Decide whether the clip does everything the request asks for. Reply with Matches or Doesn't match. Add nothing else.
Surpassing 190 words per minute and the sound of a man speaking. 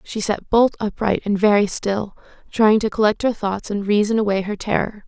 Doesn't match